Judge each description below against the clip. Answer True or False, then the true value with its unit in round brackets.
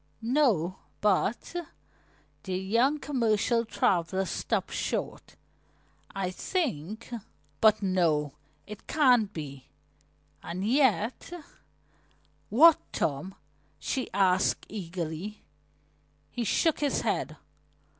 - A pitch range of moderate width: True (4.9 semitones)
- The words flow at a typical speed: False (95 wpm)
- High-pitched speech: True (205 Hz)